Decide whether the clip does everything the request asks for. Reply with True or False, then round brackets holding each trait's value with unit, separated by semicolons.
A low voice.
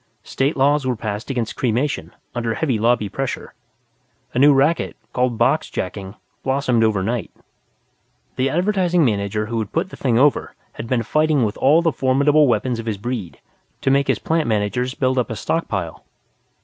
True (125 Hz)